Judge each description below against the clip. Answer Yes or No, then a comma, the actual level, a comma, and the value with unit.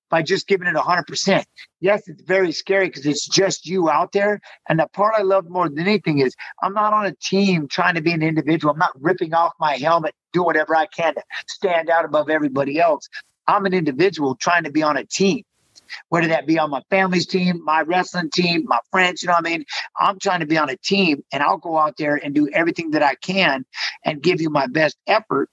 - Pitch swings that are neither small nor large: Yes, average, 3.5 semitones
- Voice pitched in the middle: Yes, medium, 170 Hz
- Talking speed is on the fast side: Yes, fast, 235 wpm